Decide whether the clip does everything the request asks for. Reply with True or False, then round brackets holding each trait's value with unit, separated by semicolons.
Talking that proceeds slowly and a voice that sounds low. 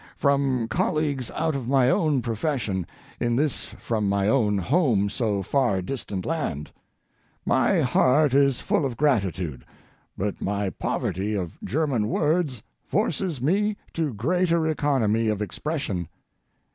True (130 wpm; 125 Hz)